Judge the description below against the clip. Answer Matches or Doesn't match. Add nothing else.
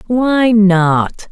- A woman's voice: Matches